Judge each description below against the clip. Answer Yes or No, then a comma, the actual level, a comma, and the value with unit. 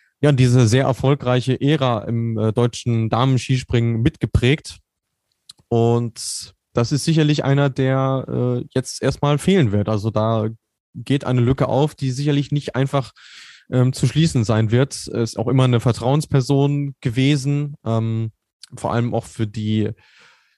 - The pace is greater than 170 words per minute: No, average, 140 wpm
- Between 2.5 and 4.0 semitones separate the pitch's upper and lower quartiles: Yes, average, 3.4 semitones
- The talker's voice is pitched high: No, low, 125 Hz